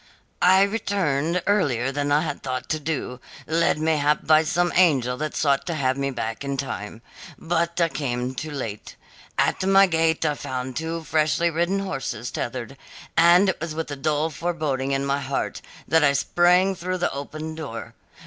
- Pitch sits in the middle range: Yes, medium, 155 Hz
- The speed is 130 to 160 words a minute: No, average, 175 wpm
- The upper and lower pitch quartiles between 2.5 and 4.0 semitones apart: Yes, average, 3.7 semitones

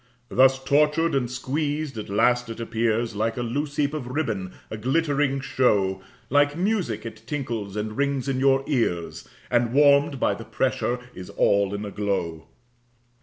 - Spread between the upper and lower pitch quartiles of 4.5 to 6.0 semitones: Yes, average, 4.8 semitones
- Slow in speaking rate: No, average, 165 wpm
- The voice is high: No, low, 125 Hz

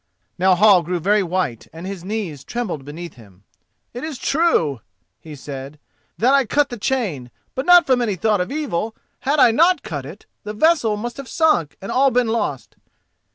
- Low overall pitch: No, high, 210 Hz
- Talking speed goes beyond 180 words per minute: Yes, average, 190 wpm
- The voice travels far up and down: Yes, wide, 7.9 semitones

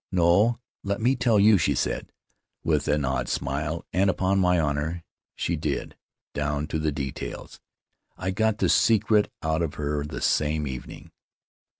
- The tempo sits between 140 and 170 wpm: Yes, average, 165 wpm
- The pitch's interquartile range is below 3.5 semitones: No, average, 5.0 semitones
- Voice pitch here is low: Yes, very low, 80 Hz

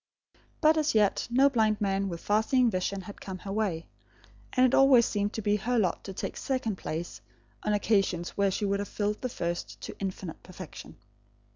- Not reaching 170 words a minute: No, average, 200 wpm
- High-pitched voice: Yes, high, 205 Hz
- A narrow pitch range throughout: No, average, 3.2 semitones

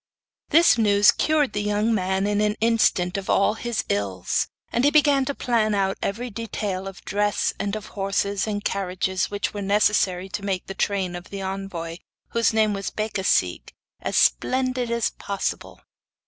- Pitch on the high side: Yes, high, 205 Hz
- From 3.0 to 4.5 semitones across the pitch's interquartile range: No, narrow, 2.6 semitones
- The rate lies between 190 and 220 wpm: No, average, 170 wpm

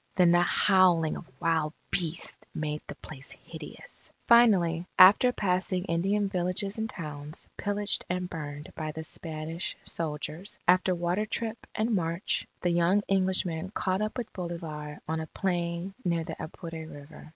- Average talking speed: Yes, average, 150 wpm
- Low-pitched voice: No, medium, 175 Hz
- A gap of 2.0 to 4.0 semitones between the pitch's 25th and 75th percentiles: Yes, average, 3.1 semitones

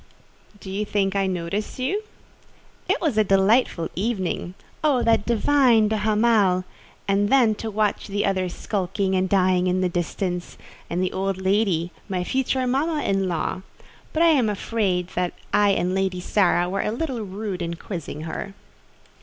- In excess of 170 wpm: No, average, 160 wpm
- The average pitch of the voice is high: Yes, high, 195 Hz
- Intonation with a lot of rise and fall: No, average, 3.2 semitones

